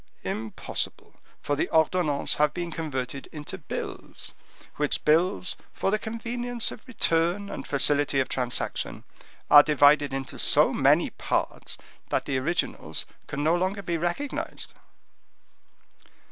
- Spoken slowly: Yes, slow, 125 wpm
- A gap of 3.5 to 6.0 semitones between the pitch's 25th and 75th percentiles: Yes, average, 4.3 semitones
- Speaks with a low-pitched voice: No, medium, 160 Hz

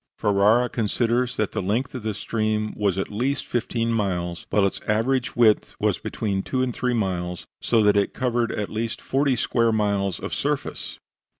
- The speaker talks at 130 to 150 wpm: No, average, 180 wpm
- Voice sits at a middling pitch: No, low, 110 Hz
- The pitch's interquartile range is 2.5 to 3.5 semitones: Yes, average, 3.1 semitones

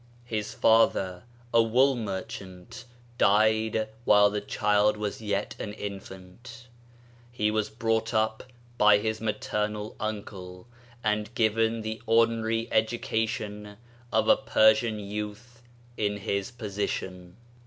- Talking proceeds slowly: Yes, slow, 115 wpm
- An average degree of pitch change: No, narrow, 1.6 semitones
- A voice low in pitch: Yes, low, 110 Hz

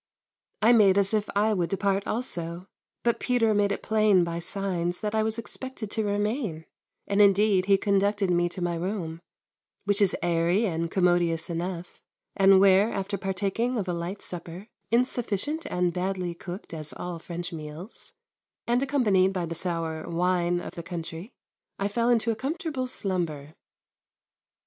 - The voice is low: No, high, 195 Hz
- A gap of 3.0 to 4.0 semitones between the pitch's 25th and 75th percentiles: Yes, average, 3.6 semitones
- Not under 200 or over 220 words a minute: No, average, 160 wpm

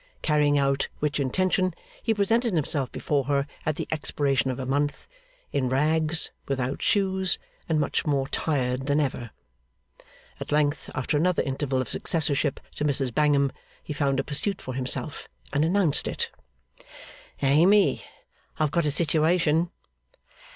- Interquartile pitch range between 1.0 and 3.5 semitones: Yes, average, 2.9 semitones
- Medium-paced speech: Yes, average, 145 wpm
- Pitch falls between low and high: Yes, medium, 145 Hz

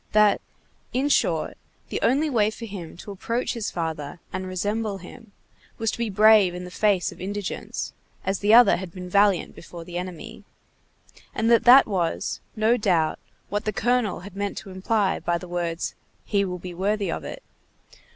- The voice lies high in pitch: Yes, high, 200 Hz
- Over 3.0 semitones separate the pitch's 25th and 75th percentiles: Yes, average, 3.4 semitones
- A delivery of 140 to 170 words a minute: No, average, 180 wpm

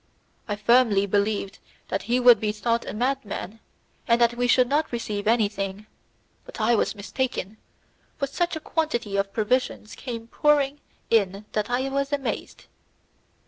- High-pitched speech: Yes, high, 235 Hz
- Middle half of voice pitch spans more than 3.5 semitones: Yes, average, 4.0 semitones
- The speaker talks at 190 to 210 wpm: No, average, 150 wpm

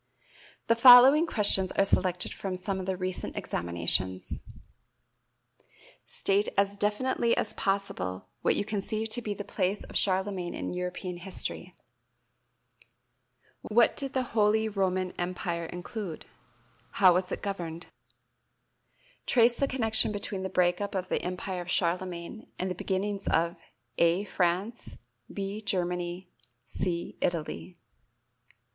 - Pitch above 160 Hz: Yes, high, 190 Hz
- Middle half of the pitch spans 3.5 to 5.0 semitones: No, average, 2.8 semitones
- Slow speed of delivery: Yes, slow, 125 wpm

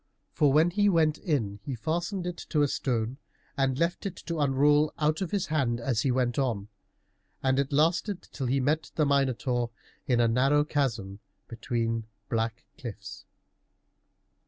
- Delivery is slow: No, average, 160 wpm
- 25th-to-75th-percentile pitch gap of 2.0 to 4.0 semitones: No, average, 4.4 semitones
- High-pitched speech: No, low, 135 Hz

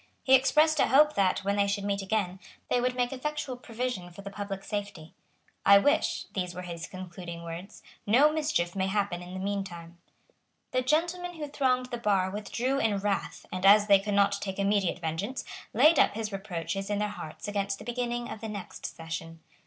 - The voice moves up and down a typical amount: Yes, average, 4.9 semitones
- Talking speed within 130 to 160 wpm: No, average, 200 wpm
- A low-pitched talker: No, high, 200 Hz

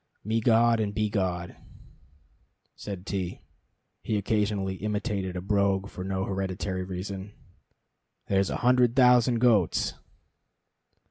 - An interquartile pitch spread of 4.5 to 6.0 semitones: No, average, 2.8 semitones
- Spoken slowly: Yes, slow, 105 wpm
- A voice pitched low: Yes, low, 100 Hz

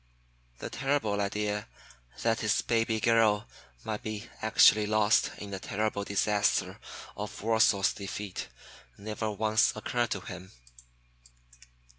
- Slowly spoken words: Yes, slow, 115 wpm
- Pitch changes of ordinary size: No, narrow, 1.4 semitones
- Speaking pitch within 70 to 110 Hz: Yes, low, 105 Hz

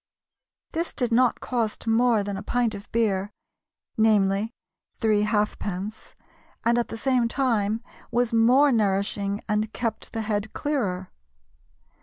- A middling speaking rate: No, slow, 130 wpm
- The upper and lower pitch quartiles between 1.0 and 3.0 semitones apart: Yes, average, 2.7 semitones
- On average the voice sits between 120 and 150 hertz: No, high, 220 Hz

